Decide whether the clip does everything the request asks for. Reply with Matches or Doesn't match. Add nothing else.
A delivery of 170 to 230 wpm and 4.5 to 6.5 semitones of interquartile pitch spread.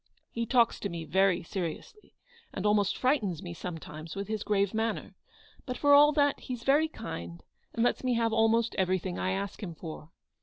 Matches